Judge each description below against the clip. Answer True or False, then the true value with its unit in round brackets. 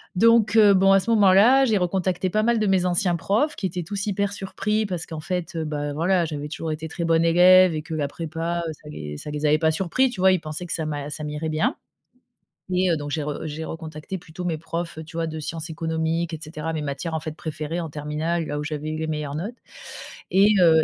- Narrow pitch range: False (3.3 semitones)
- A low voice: False (165 Hz)